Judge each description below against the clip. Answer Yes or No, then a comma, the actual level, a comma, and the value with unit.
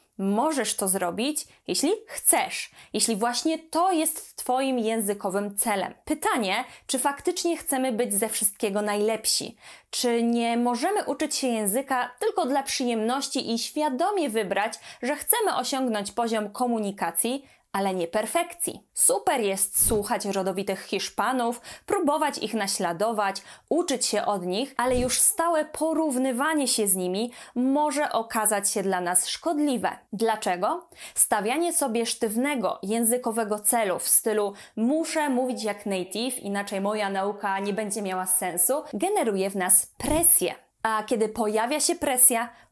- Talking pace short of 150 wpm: Yes, average, 130 wpm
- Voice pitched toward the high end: Yes, high, 235 Hz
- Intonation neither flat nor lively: No, wide, 5.8 semitones